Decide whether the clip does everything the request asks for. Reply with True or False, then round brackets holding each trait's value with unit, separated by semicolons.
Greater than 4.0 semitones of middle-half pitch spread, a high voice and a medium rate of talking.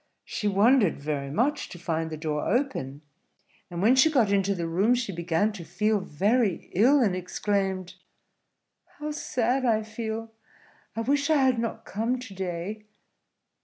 True (5.6 semitones; 210 Hz; 160 wpm)